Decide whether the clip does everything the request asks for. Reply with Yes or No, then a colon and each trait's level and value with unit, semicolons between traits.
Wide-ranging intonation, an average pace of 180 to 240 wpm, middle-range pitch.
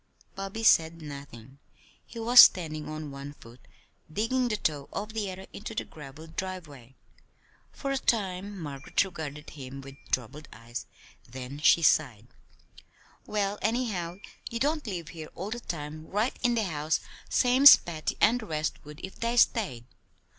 No: wide, 6.7 semitones; average, 155 wpm; medium, 170 Hz